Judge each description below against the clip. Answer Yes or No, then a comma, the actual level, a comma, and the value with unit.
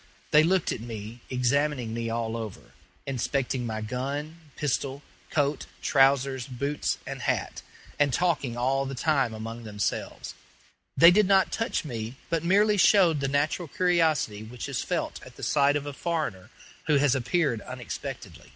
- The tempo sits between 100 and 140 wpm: No, average, 155 wpm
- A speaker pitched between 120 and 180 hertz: Yes, medium, 140 Hz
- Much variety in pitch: No, average, 4.6 semitones